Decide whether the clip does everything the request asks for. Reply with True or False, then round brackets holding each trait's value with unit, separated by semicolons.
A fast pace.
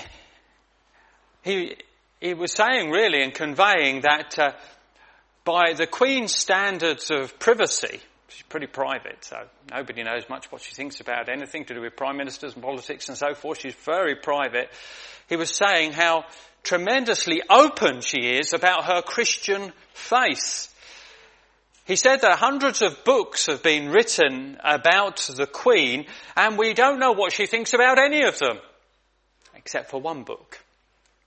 False (150 wpm)